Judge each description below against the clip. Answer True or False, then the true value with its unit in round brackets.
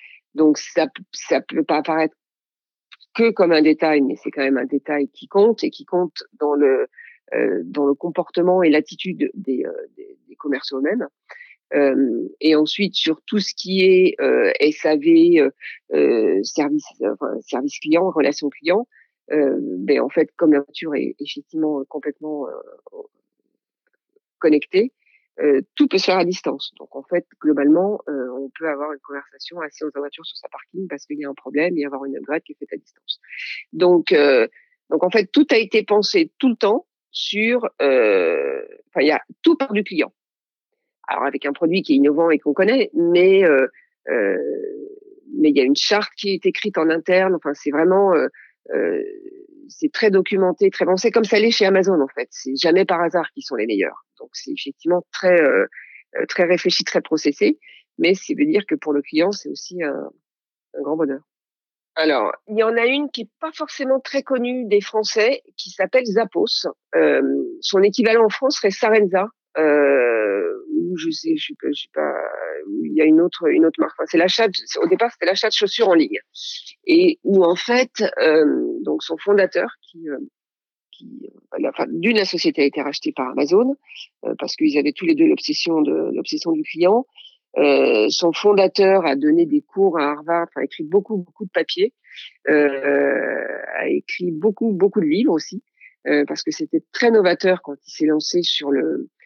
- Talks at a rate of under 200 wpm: True (190 wpm)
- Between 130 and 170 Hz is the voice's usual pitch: False (210 Hz)